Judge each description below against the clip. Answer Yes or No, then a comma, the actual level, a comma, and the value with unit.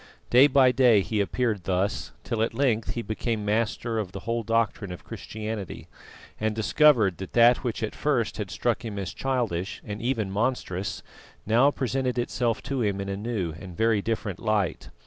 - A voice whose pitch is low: Yes, low, 110 Hz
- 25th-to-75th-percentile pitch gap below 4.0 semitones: Yes, average, 3.1 semitones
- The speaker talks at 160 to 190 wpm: Yes, average, 180 wpm